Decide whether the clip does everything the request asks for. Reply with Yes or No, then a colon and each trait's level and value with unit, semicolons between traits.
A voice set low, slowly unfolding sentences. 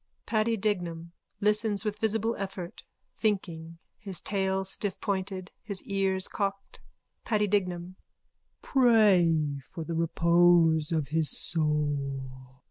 No: medium, 185 Hz; slow, 105 wpm